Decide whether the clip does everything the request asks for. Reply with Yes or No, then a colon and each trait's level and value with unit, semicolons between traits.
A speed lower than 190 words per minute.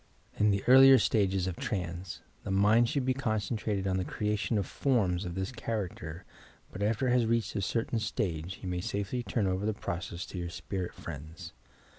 No: average, 195 wpm